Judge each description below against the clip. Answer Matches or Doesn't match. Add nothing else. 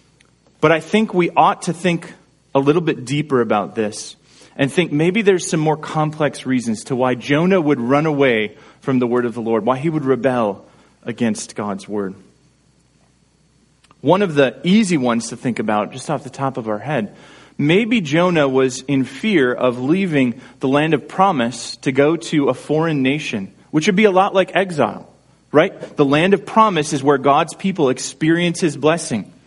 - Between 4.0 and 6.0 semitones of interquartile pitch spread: Matches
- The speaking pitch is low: Doesn't match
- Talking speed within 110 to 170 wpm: Doesn't match